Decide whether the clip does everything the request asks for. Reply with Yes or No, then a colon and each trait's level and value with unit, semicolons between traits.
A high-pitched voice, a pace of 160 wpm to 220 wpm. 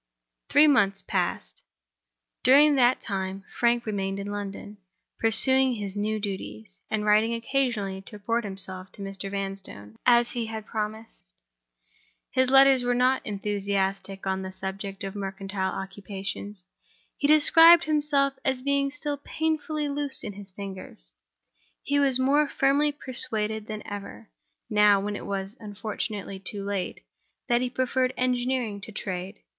No: high, 215 Hz; average, 140 wpm